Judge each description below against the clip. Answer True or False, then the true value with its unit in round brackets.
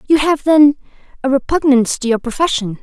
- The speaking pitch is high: True (270 Hz)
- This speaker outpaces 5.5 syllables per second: True (6.0 syllables/s)